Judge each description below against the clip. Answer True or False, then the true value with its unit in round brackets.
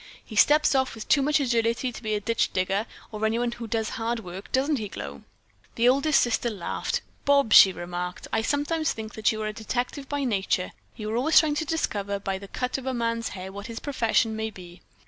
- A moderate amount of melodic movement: True (4.3 semitones)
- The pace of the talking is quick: True (225 wpm)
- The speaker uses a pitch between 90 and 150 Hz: False (230 Hz)